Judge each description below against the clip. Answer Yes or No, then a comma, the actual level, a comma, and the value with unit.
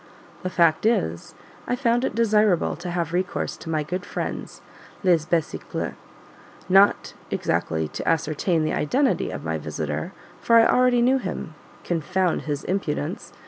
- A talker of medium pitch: Yes, medium, 180 Hz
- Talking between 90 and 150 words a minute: Yes, average, 145 wpm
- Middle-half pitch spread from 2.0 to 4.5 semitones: No, wide, 5.5 semitones